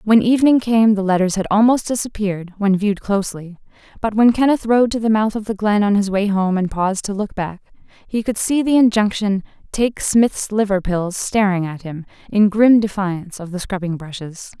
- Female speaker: Yes, female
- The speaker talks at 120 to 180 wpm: No, average, 200 wpm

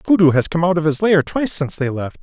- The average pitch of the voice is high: No, medium, 165 Hz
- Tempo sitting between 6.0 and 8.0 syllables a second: Yes, 6.8 syllables/s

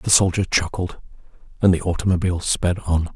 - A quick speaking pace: No, average, 150 wpm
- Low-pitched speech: Yes, very low, 90 Hz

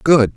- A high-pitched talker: No, low, 135 Hz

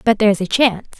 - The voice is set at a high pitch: Yes, high, 215 Hz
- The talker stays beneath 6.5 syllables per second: No, 7.4 syllables/s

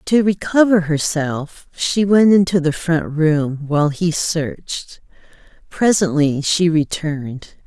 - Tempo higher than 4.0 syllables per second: No, 3.7 syllables/s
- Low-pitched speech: No, medium, 165 Hz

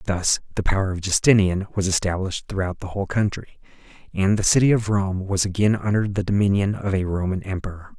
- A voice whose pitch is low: Yes, very low, 95 Hz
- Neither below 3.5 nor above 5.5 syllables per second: No, 6.0 syllables/s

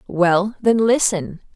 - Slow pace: Yes, slow, 115 wpm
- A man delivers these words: No, female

